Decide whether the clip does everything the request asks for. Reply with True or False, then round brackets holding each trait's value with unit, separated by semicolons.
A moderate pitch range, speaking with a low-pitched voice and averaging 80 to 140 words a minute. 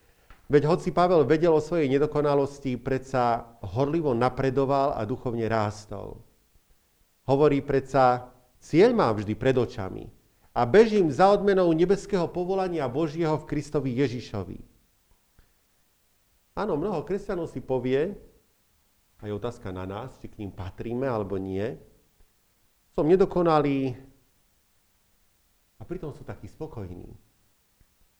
False (6.1 semitones; 130 Hz; 110 wpm)